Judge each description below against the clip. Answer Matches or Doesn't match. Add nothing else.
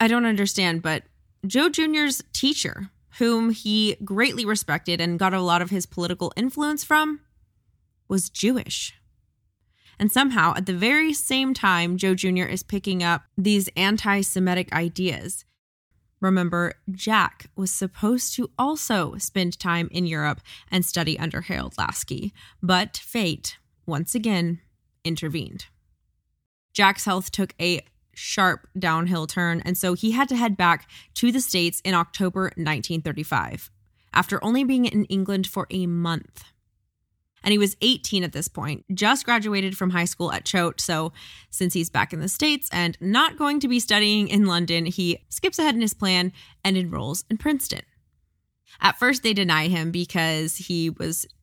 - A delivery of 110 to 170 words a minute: Matches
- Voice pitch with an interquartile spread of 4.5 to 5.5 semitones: Doesn't match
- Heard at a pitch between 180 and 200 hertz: Matches